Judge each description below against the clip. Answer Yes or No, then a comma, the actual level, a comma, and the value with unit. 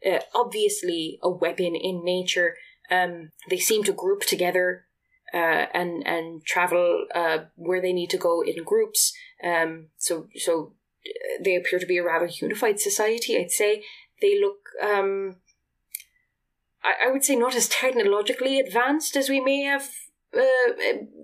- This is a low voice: No, very high, 250 Hz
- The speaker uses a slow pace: No, average, 150 wpm